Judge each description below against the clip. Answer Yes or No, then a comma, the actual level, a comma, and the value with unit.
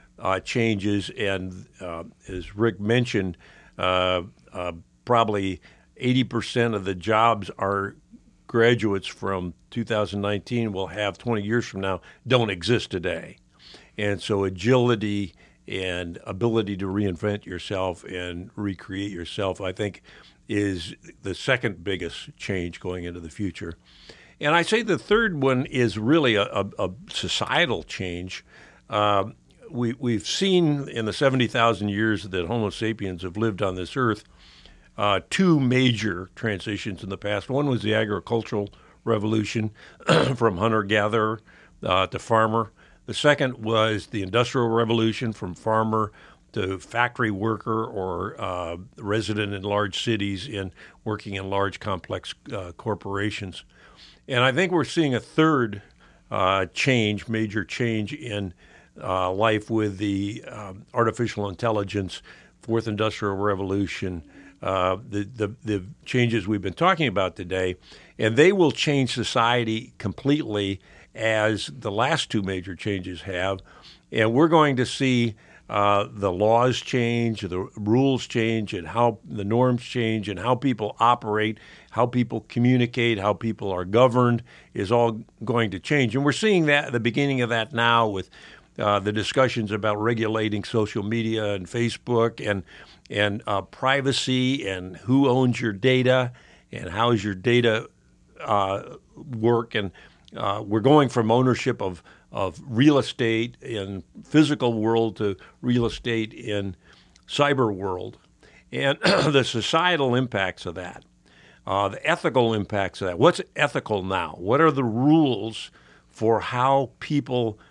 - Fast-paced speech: No, average, 140 wpm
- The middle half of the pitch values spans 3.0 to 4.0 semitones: Yes, average, 3.6 semitones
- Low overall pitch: Yes, low, 110 Hz